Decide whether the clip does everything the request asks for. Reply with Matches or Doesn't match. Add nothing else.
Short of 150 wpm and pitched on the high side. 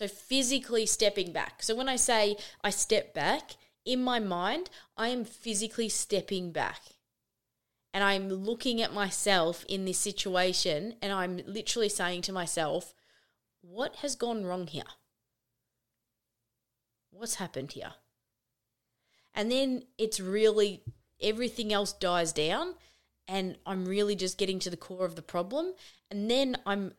Matches